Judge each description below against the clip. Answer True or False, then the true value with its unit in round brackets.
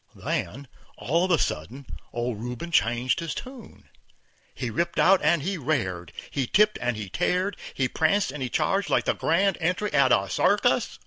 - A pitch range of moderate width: False (6.8 semitones)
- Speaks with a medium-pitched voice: True (145 Hz)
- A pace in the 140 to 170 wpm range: False (180 wpm)